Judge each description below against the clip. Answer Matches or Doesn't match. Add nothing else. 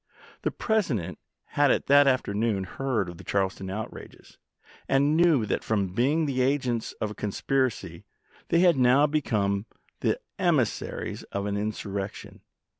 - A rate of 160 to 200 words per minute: Doesn't match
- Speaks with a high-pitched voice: Doesn't match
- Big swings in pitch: Matches